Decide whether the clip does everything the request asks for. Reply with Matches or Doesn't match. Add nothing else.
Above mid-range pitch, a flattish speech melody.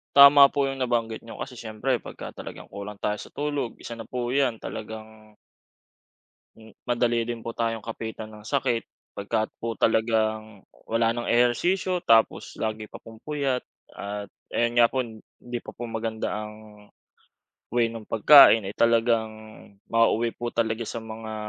Doesn't match